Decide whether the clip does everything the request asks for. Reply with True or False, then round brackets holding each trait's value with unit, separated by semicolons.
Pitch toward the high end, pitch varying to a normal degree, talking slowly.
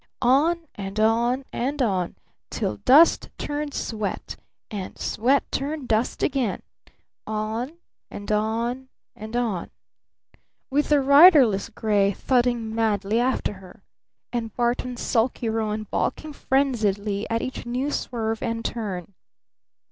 True (230 Hz; 3.6 semitones; 120 wpm)